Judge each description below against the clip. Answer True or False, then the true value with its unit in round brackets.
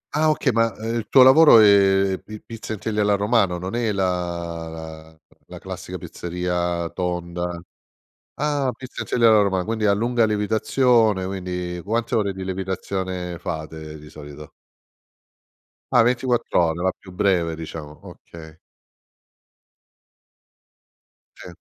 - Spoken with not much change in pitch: False (4.3 semitones)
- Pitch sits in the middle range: False (95 Hz)